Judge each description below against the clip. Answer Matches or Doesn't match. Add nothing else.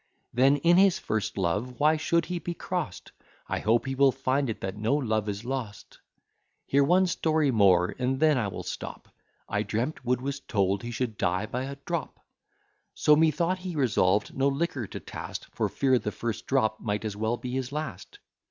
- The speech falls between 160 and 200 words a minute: Matches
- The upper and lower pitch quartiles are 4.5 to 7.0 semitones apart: Matches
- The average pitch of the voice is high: Doesn't match